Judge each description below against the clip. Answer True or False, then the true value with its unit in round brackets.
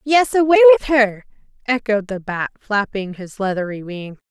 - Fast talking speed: False (155 wpm)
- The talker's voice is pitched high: True (215 Hz)